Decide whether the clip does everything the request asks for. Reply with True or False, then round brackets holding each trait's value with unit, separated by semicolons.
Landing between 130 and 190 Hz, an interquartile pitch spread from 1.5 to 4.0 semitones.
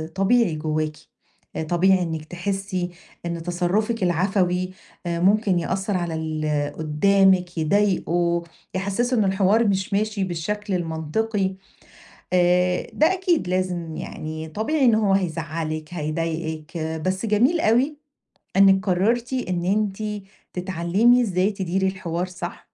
True (185 Hz; 3.4 semitones)